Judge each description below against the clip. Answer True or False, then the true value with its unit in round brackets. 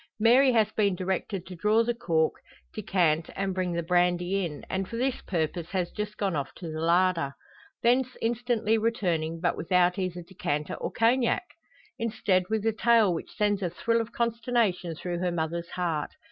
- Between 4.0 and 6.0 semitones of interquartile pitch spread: True (4.6 semitones)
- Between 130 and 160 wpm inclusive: False (175 wpm)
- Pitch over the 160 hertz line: True (185 Hz)